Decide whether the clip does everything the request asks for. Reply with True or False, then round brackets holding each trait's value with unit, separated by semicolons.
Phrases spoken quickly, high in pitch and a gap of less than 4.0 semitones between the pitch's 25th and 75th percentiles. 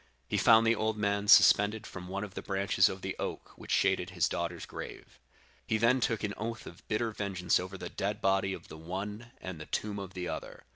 False (225 wpm; 100 Hz; 2.5 semitones)